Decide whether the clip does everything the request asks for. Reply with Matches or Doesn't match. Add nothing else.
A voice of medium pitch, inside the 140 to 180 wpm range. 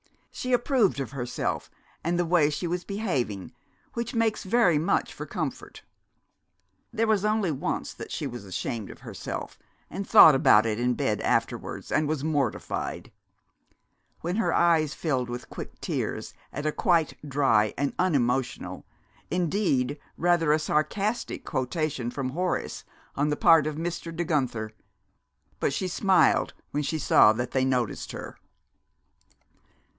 Matches